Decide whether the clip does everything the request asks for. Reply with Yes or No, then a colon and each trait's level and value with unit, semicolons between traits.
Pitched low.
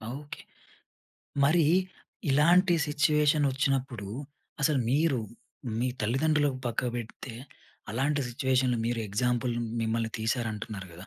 Yes: low, 130 Hz